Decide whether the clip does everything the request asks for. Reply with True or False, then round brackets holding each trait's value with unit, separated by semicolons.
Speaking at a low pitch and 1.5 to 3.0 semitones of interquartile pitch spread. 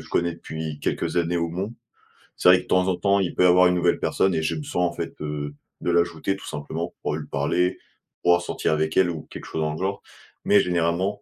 True (85 Hz; 2.5 semitones)